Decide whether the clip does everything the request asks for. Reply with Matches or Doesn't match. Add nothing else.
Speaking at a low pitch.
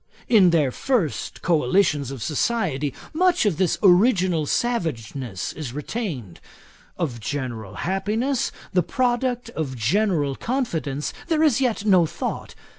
Doesn't match